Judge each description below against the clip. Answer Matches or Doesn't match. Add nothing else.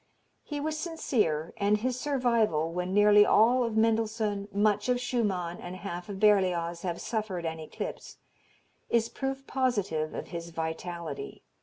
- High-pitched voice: Matches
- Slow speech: Doesn't match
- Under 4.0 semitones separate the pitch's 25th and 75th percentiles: Doesn't match